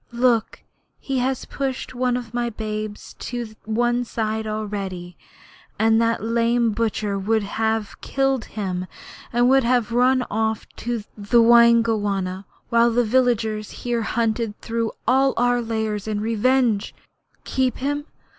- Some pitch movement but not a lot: No, narrow, 2.1 semitones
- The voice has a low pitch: No, high, 230 Hz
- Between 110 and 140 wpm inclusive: Yes, slow, 135 wpm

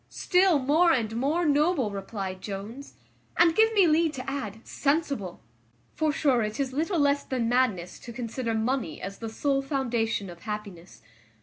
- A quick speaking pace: No, average, 165 wpm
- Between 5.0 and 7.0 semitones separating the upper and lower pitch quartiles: Yes, wide, 5.6 semitones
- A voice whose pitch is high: Yes, very high, 255 Hz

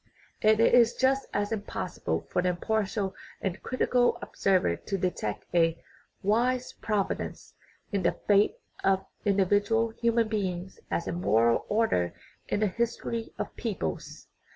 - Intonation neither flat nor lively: Yes, average, 3.9 semitones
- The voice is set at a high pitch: Yes, high, 205 Hz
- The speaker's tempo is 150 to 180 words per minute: Yes, average, 155 wpm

